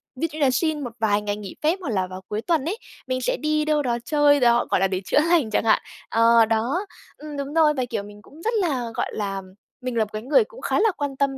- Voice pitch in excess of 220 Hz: Yes, very high, 260 Hz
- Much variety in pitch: Yes, wide, 5.8 semitones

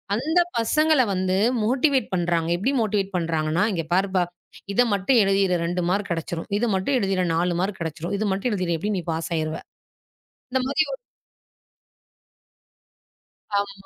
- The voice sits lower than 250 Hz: Yes, high, 195 Hz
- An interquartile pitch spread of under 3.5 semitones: No, average, 3.8 semitones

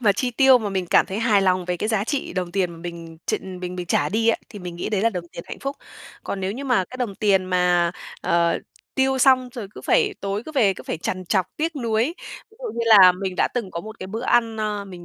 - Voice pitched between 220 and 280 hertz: No, high, 200 Hz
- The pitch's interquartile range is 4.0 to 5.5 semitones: Yes, average, 4.5 semitones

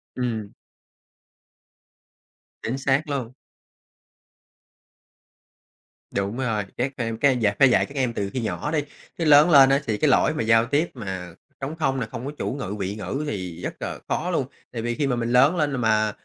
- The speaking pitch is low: Yes, low, 125 Hz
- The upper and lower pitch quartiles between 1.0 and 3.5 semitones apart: No, average, 4.2 semitones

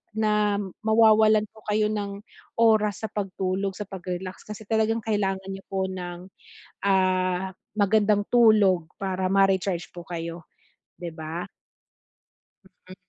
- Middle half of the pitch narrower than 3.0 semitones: Yes, narrow, 2.5 semitones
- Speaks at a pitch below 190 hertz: No, high, 195 Hz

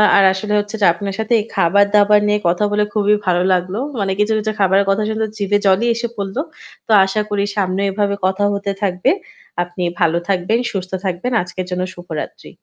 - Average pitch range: No, narrow, 2.2 semitones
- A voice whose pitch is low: No, high, 200 Hz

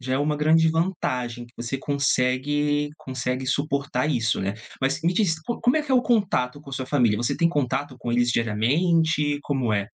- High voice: No, medium, 140 Hz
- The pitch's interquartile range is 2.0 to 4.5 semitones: Yes, average, 4.2 semitones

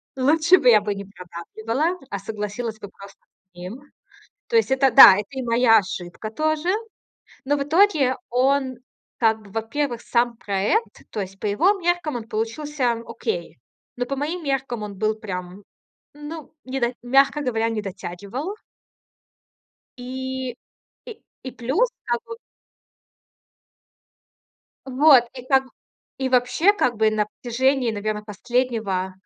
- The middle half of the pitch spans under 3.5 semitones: No, average, 4.8 semitones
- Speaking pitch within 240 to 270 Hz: Yes, high, 245 Hz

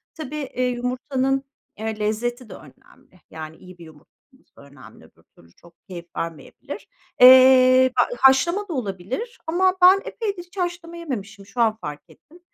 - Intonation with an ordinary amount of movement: No, wide, 9.0 semitones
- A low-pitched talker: No, very high, 255 Hz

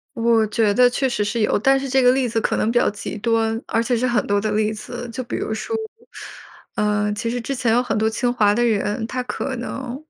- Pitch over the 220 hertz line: Yes, high, 230 Hz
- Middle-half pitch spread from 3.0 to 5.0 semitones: No, narrow, 2.5 semitones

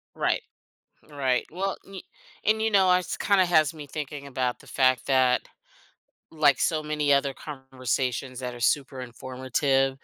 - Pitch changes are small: No, average, 3.2 semitones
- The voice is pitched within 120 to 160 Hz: Yes, medium, 140 Hz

